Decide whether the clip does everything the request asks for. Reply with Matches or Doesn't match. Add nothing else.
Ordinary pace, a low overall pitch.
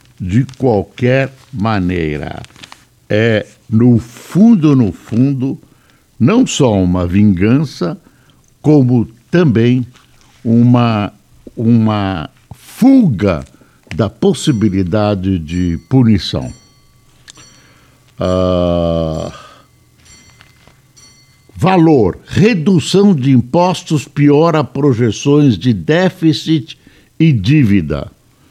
Doesn't match